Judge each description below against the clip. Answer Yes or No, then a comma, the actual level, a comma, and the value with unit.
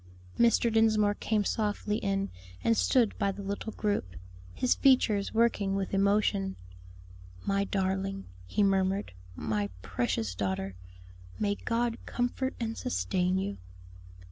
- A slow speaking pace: Yes, slow, 120 wpm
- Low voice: No, high, 200 Hz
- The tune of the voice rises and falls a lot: No, narrow, 2.5 semitones